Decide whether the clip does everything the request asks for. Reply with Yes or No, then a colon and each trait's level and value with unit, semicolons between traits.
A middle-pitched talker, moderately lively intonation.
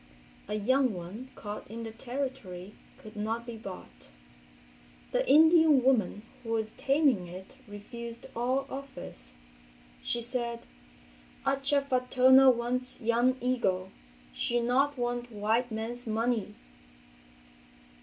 No: high, 240 Hz; average, 3.2 semitones